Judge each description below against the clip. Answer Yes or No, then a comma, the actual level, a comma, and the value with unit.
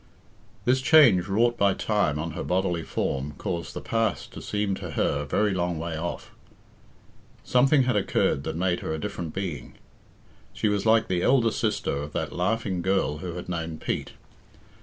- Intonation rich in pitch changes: No, average, 4.7 semitones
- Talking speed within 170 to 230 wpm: Yes, average, 180 wpm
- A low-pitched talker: Yes, very low, 95 Hz